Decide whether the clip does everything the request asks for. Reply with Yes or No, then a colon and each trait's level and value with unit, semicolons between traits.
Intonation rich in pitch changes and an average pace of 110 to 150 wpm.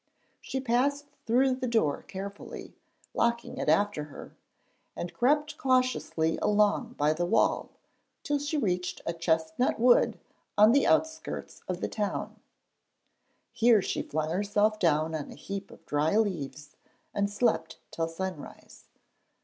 Yes: wide, 7.1 semitones; slow, 135 wpm